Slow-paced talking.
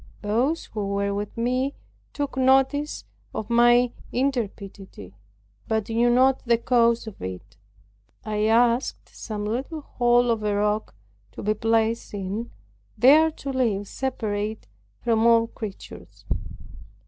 Yes: slow, 125 wpm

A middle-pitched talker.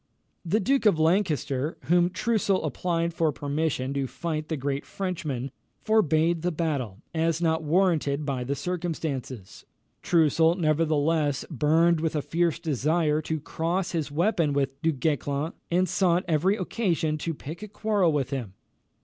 Yes: medium, 160 Hz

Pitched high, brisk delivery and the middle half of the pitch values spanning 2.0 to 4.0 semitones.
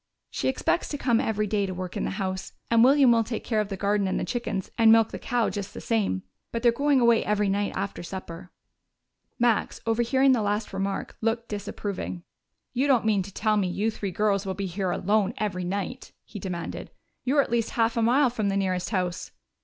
Yes: high, 210 Hz; fast, 215 wpm; average, 3.2 semitones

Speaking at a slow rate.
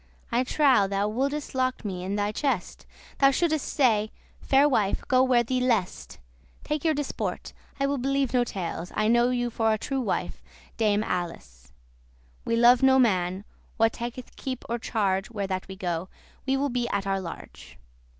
No: average, 185 wpm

